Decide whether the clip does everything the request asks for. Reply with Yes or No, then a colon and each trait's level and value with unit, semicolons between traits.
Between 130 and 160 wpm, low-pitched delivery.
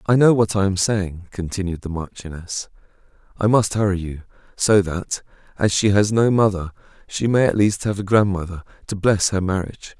No: average, 185 wpm; low, 100 Hz